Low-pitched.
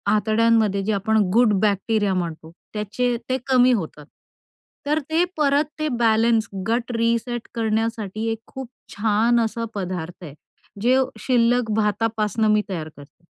No: high, 220 Hz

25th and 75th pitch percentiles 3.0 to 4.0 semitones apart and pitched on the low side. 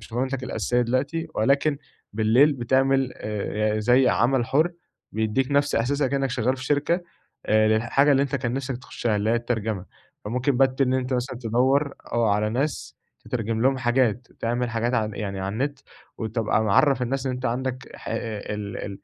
Yes: average, 3.3 semitones; low, 125 Hz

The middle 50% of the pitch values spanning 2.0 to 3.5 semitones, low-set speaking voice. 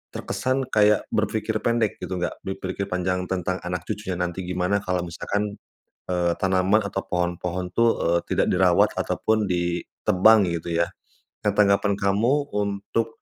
Yes: average, 2.8 semitones; very low, 95 Hz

